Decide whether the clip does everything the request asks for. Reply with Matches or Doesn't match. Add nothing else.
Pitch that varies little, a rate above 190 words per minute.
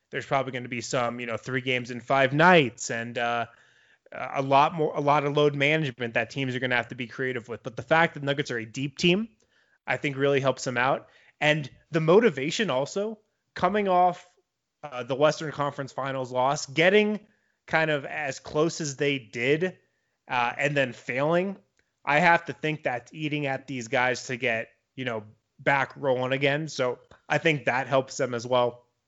Doesn't match